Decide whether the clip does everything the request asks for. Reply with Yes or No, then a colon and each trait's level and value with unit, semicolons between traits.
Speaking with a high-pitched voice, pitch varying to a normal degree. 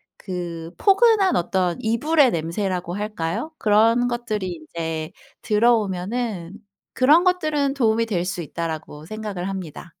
No: high, 205 Hz; wide, 5.8 semitones